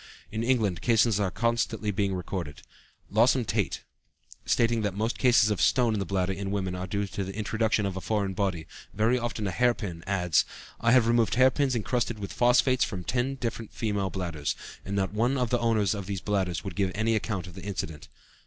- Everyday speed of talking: No, fast, 210 wpm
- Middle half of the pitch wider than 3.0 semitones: Yes, average, 3.5 semitones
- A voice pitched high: No, low, 105 Hz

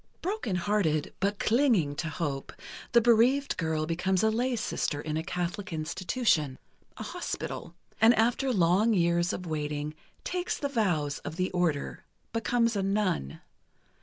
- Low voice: No, medium, 185 Hz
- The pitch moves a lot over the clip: Yes, wide, 6.3 semitones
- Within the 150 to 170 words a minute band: No, slow, 135 wpm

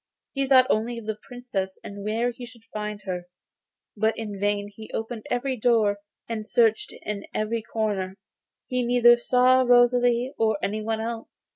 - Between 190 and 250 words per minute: No, average, 160 wpm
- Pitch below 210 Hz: No, high, 225 Hz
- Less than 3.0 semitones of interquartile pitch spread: Yes, narrow, 2.5 semitones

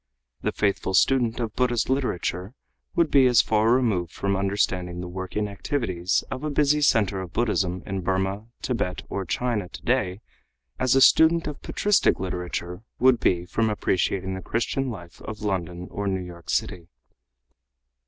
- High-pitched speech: No, low, 100 Hz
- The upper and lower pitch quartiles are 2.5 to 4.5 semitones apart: No, average, 5.1 semitones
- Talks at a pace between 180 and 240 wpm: No, average, 155 wpm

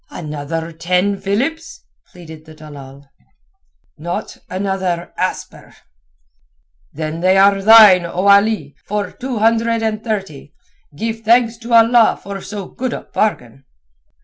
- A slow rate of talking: Yes, slow, 120 wpm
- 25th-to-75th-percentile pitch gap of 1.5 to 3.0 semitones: No, average, 5.3 semitones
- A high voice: Yes, high, 195 Hz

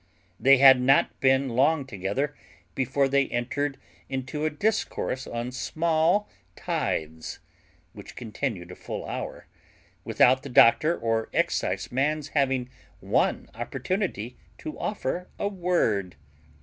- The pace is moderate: No, slow, 115 wpm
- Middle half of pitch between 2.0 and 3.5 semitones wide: No, average, 4.1 semitones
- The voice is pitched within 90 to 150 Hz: Yes, low, 135 Hz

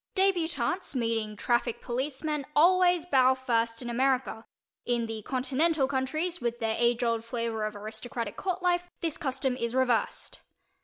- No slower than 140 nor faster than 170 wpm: Yes, average, 145 wpm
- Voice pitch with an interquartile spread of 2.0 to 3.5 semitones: No, average, 5.2 semitones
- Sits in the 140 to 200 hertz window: No, very high, 255 Hz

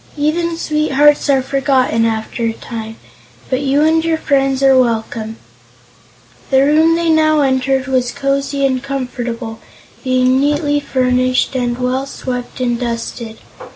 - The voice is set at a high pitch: Yes, very high, 265 Hz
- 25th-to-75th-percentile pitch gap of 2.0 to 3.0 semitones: Yes, narrow, 2.6 semitones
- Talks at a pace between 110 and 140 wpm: Yes, slow, 135 wpm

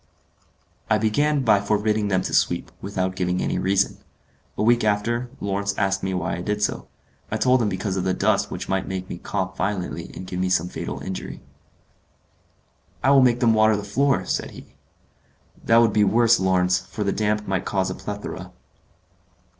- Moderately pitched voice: No, low, 100 Hz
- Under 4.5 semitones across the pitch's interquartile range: Yes, average, 2.7 semitones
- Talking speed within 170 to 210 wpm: Yes, average, 185 wpm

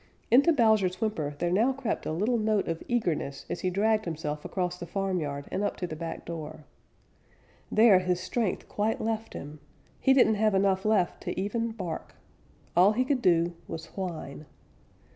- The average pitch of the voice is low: No, high, 190 Hz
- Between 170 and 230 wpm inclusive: Yes, average, 175 wpm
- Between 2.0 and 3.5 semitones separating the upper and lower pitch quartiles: No, average, 4.6 semitones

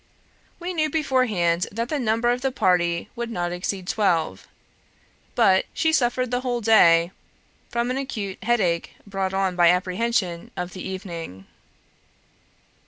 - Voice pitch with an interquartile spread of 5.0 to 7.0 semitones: Yes, wide, 5.5 semitones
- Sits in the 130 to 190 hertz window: No, high, 200 Hz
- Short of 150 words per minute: Yes, average, 140 wpm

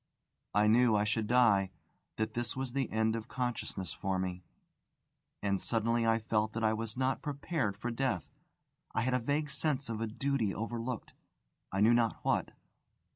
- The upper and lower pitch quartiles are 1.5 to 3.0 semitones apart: Yes, average, 2.7 semitones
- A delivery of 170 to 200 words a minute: Yes, average, 175 wpm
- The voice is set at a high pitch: No, low, 115 Hz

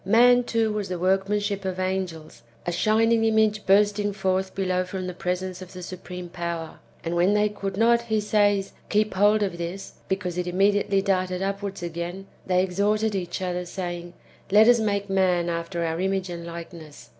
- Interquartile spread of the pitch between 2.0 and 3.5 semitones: Yes, narrow, 2.5 semitones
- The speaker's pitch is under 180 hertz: No, high, 190 Hz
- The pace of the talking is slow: No, average, 185 wpm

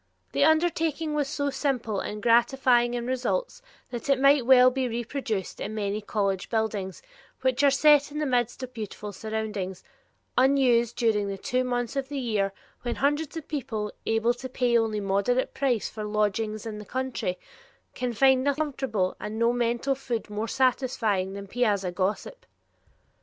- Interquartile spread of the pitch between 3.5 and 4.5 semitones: Yes, average, 4.0 semitones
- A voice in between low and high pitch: No, high, 240 Hz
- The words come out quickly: No, average, 170 wpm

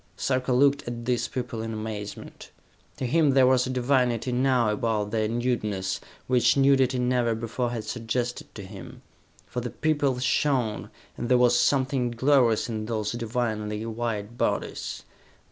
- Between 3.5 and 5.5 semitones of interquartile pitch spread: No, narrow, 2.5 semitones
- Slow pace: No, average, 150 wpm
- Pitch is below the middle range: Yes, low, 120 Hz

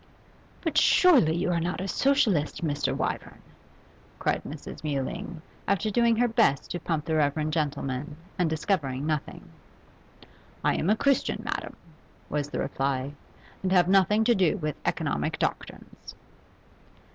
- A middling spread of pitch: No, wide, 5.7 semitones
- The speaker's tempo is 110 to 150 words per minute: Yes, average, 140 wpm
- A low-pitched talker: No, medium, 170 Hz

